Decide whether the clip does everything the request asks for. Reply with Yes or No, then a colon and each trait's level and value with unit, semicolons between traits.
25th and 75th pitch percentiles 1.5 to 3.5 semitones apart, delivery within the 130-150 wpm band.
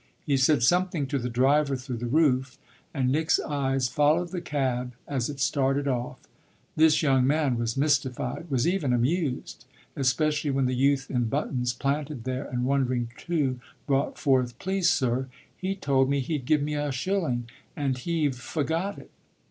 No: average, 3.1 semitones; average, 165 wpm